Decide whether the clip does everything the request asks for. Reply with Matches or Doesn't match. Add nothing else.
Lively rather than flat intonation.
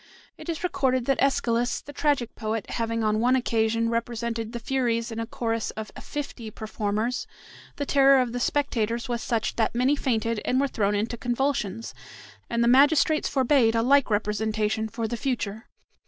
Doesn't match